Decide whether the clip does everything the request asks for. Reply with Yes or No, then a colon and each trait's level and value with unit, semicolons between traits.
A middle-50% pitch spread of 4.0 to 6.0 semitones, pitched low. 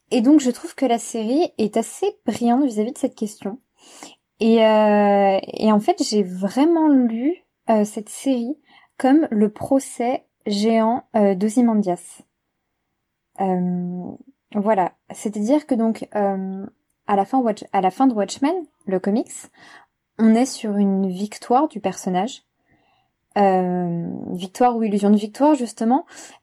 No: average, 4.6 semitones; high, 225 Hz